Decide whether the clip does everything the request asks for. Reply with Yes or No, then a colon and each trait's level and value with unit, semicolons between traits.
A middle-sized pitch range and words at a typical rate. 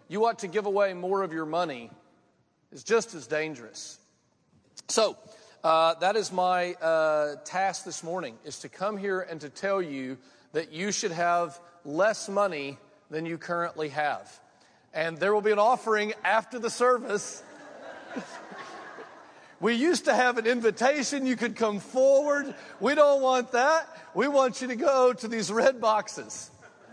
No: wide, 6.4 semitones; average, 160 wpm